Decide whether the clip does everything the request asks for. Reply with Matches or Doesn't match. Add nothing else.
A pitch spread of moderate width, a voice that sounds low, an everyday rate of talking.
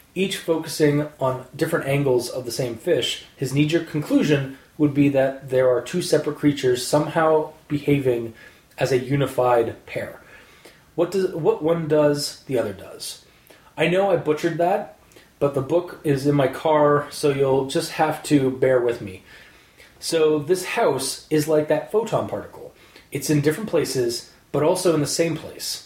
Doesn't match